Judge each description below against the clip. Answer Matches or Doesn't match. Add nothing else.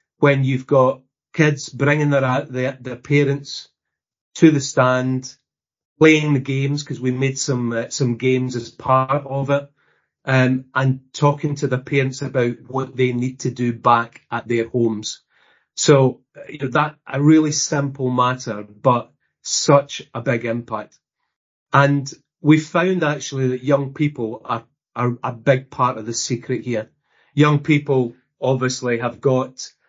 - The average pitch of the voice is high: Doesn't match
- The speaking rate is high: Doesn't match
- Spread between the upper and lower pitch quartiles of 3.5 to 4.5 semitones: Doesn't match